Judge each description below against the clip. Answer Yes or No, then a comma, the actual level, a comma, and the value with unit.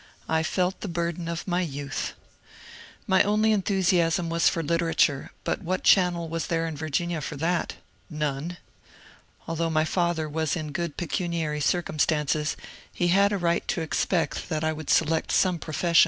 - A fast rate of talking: No, average, 160 wpm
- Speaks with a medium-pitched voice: Yes, medium, 165 Hz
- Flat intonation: Yes, narrow, 2.1 semitones